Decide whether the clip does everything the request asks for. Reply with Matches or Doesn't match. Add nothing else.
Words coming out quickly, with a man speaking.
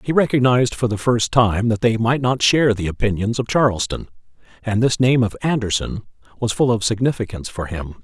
Doesn't match